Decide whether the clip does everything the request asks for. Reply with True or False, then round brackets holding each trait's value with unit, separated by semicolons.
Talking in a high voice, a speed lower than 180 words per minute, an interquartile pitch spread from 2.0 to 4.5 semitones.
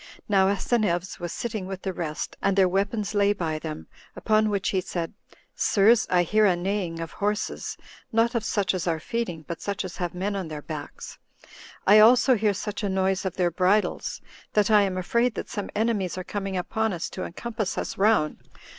False (195 Hz; 200 wpm; 3.1 semitones)